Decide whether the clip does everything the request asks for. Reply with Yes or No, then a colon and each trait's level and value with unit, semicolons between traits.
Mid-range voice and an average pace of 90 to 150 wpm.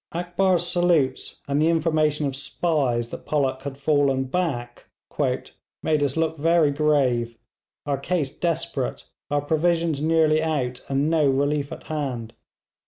Yes: medium, 150 Hz; slow, 135 wpm